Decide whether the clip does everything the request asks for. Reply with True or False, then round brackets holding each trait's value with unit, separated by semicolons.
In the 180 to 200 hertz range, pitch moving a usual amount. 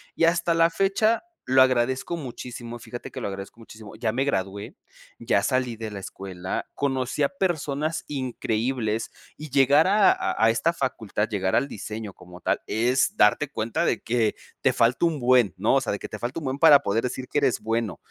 False (125 Hz; 4.5 semitones)